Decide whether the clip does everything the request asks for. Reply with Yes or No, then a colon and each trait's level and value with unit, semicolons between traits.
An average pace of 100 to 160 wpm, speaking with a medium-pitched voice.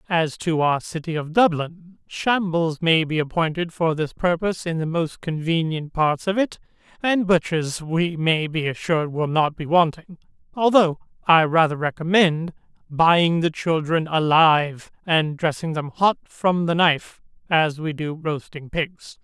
Yes: average, 155 wpm; medium, 165 Hz